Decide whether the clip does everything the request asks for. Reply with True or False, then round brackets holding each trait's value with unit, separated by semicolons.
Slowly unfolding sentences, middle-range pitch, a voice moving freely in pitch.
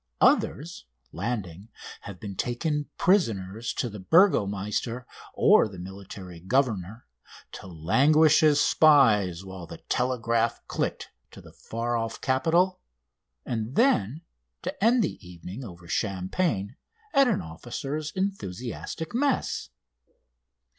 False (115 wpm; 115 Hz; 8.0 semitones)